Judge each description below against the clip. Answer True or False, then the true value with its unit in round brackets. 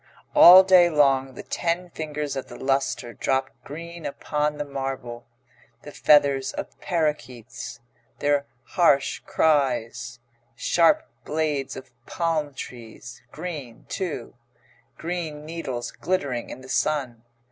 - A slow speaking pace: True (115 wpm)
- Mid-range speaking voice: True (145 Hz)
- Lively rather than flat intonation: False (3.9 semitones)